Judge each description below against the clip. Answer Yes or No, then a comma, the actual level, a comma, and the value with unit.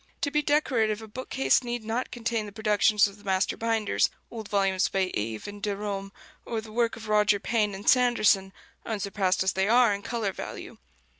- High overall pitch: Yes, high, 210 Hz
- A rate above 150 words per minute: Yes, average, 190 wpm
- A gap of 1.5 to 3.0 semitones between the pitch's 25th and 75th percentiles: Yes, narrow, 2.5 semitones